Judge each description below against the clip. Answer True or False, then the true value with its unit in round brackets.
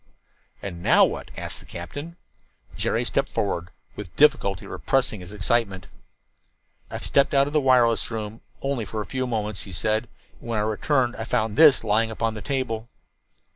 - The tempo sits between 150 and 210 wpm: True (170 wpm)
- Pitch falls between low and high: False (110 Hz)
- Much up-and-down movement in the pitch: False (3.8 semitones)